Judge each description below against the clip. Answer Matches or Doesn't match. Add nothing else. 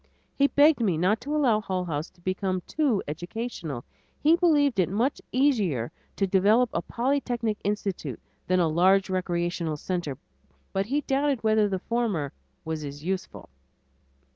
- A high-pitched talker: Matches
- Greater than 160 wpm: Doesn't match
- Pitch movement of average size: Doesn't match